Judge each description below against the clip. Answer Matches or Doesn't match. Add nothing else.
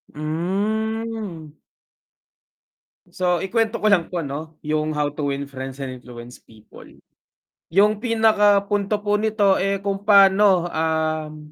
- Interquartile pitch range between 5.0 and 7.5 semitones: Matches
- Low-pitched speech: Doesn't match